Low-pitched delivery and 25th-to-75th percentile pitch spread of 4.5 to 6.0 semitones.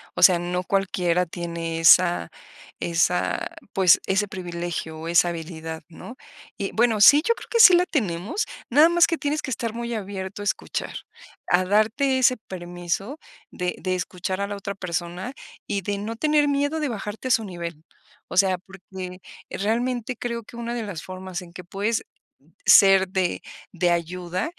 No: high, 190 Hz; average, 4.9 semitones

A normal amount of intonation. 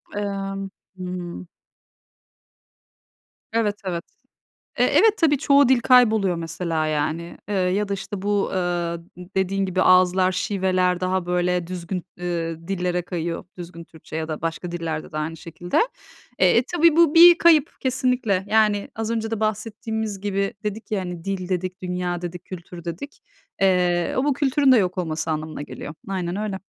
Yes: average, 3.5 semitones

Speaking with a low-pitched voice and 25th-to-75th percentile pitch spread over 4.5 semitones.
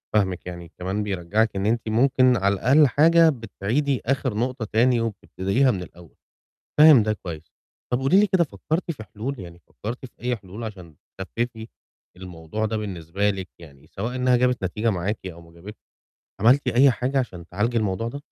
Yes: low, 110 Hz; average, 5.1 semitones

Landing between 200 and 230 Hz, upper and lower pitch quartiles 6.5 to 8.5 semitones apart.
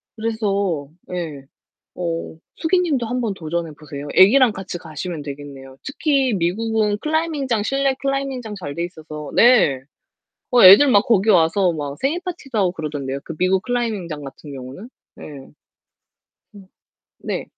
No: high, 190 Hz; wide, 7.7 semitones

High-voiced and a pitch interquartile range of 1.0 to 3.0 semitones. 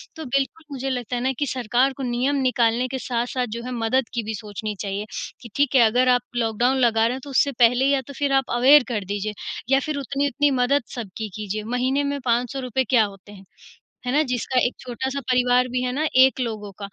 Yes: very high, 250 Hz; average, 2.7 semitones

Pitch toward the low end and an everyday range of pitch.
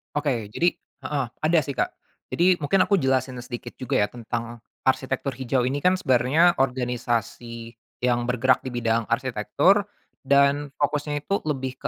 Yes: low, 130 Hz; average, 3.4 semitones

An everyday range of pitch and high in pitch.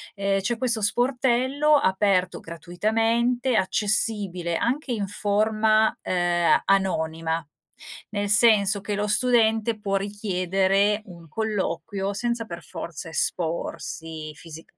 Yes: average, 4.1 semitones; high, 200 Hz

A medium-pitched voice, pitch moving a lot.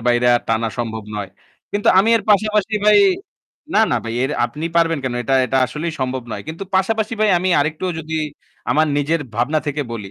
Yes: medium, 155 Hz; wide, 7.6 semitones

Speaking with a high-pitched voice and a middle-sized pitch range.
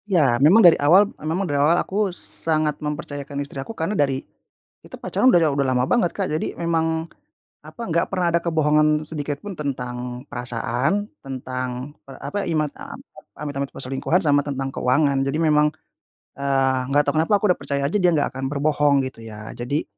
No: medium, 145 Hz; average, 3.2 semitones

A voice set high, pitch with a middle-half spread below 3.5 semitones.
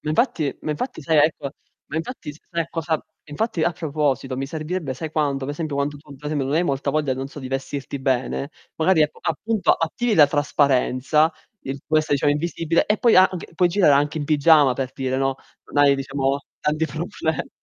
No: medium, 150 Hz; average, 2.7 semitones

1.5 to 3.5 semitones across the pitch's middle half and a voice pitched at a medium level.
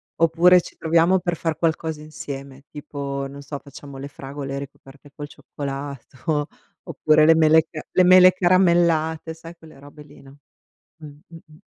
Yes: average, 2.7 semitones; medium, 155 Hz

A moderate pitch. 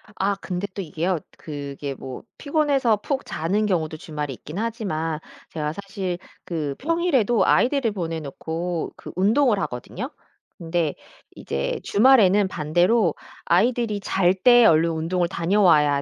Yes: medium, 180 Hz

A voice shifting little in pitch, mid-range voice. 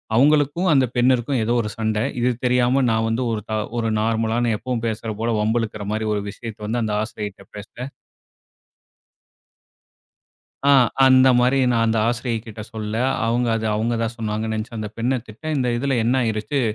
No: narrow, 2.3 semitones; low, 115 Hz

